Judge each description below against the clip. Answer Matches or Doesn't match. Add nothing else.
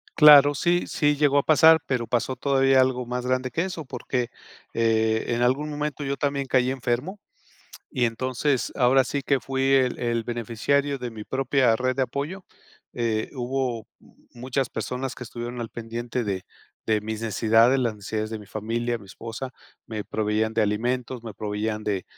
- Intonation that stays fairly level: Doesn't match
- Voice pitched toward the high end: Doesn't match